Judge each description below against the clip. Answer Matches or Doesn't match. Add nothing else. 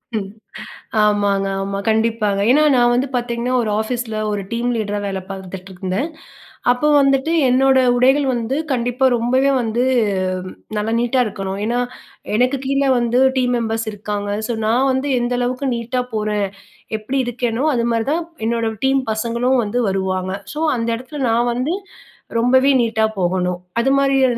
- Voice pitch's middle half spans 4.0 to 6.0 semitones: Doesn't match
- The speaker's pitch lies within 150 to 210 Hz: Doesn't match